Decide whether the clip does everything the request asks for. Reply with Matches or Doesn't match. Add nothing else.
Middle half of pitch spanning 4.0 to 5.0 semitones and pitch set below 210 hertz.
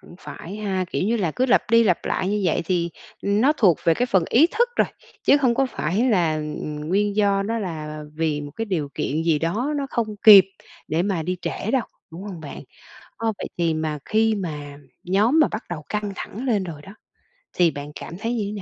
Doesn't match